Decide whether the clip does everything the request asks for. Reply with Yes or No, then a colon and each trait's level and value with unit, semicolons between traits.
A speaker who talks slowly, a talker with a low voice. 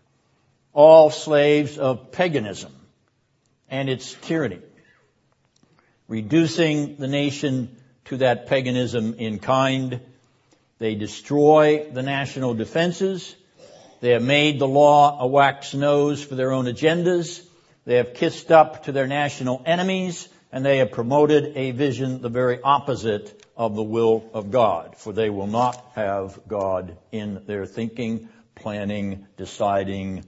Yes: slow, 130 wpm; low, 130 Hz